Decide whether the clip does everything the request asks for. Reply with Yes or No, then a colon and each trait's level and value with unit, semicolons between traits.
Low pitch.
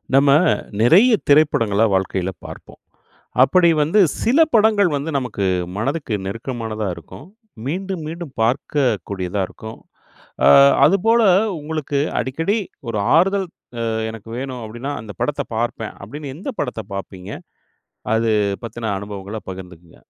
Yes: low, 125 Hz